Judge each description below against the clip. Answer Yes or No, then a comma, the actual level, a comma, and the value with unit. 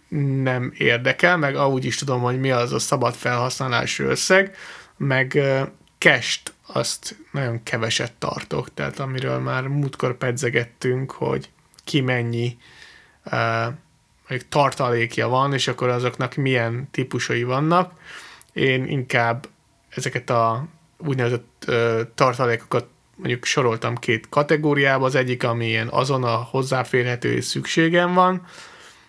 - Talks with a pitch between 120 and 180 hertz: Yes, low, 130 Hz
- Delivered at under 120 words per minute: Yes, average, 110 wpm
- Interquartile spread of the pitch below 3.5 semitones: Yes, average, 2.7 semitones